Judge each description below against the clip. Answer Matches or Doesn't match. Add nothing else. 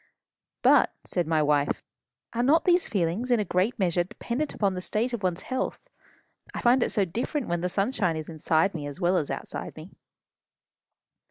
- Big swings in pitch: Matches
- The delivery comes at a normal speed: Matches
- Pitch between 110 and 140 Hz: Doesn't match